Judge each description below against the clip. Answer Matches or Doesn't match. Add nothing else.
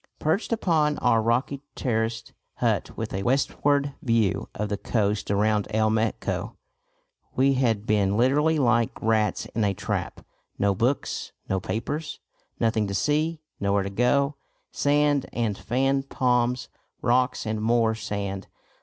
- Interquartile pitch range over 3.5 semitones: Matches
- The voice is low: Matches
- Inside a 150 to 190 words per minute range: Doesn't match